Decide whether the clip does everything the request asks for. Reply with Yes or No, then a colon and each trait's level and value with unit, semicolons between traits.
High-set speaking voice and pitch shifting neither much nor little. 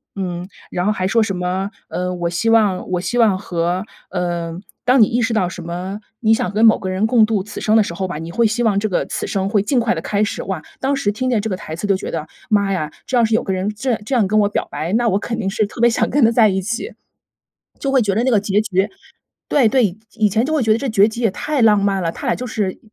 Yes: high, 205 Hz; average, 3.4 semitones